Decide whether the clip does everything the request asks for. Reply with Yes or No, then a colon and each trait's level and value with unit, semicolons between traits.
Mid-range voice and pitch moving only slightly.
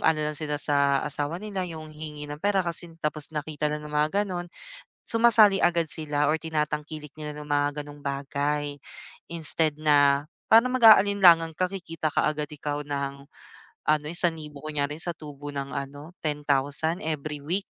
Yes: medium, 150 Hz; narrow, 2.3 semitones